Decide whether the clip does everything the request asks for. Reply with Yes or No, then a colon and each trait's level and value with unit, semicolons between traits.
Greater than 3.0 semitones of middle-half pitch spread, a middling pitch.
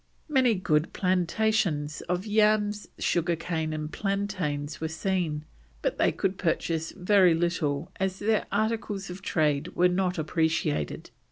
Yes: average, 4.3 semitones; medium, 180 Hz